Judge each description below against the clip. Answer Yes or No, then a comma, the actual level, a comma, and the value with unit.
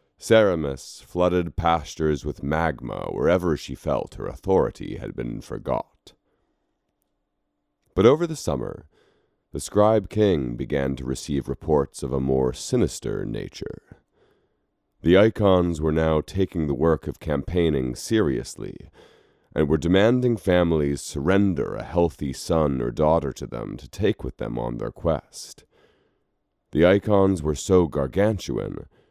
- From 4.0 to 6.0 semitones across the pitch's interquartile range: Yes, average, 5.0 semitones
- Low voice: Yes, very low, 80 Hz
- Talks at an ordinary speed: No, slow, 130 wpm